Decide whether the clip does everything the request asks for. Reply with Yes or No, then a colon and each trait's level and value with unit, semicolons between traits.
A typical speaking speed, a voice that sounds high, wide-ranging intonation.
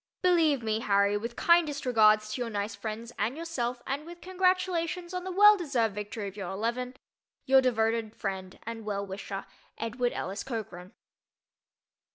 Yes: average, 160 wpm; high, 230 Hz; wide, 6.8 semitones